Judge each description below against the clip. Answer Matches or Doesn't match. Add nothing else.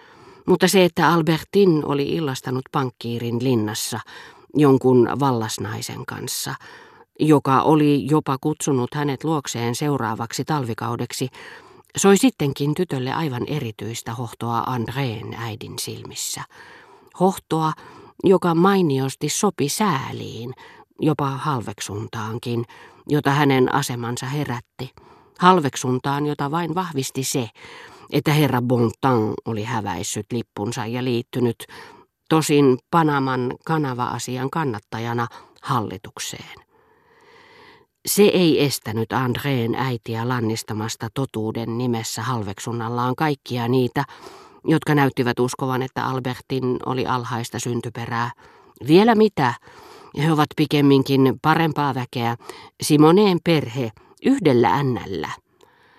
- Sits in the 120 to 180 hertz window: Matches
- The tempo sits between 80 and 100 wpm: Matches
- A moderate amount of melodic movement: Matches